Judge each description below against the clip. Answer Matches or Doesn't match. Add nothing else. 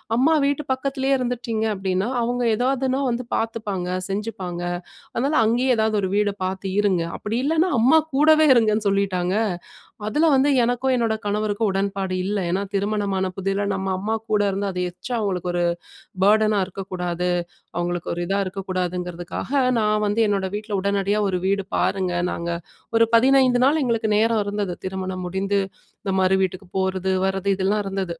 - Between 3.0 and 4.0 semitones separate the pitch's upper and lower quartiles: Matches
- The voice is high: Matches